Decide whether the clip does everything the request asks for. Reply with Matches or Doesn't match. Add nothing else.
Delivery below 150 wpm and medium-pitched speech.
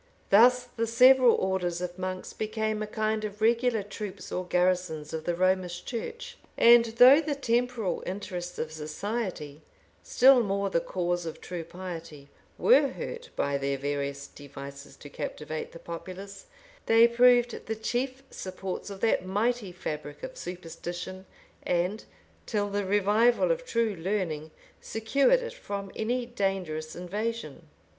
Doesn't match